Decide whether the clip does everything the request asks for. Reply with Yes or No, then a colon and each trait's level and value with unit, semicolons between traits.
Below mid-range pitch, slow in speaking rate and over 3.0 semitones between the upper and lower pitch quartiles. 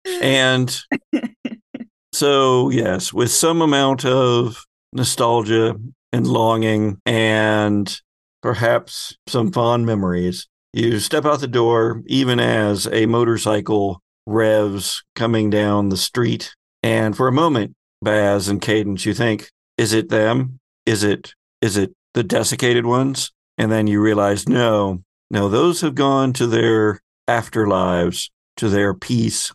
Yes: low, 115 Hz; slow, 130 wpm; average, 3.6 semitones